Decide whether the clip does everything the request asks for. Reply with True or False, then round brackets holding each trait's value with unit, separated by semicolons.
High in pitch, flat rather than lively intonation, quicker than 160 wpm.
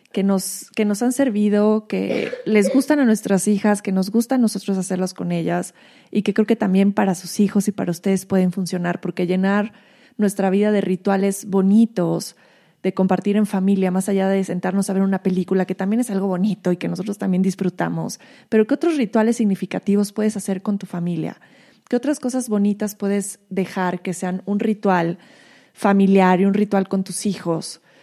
True (195 Hz; 2.3 semitones; 190 wpm)